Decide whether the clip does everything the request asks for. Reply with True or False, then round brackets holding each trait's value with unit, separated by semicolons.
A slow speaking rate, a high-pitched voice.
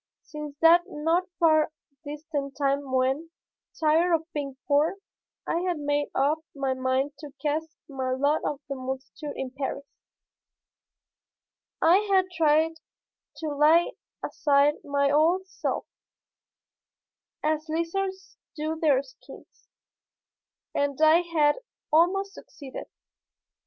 True (115 wpm; 300 Hz)